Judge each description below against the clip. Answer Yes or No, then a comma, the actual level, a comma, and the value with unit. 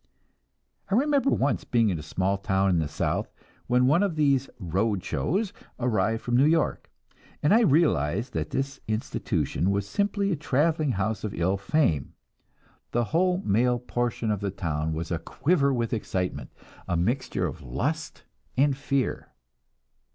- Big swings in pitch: Yes, wide, 7.3 semitones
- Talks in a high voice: No, low, 120 Hz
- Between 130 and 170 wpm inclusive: Yes, average, 160 wpm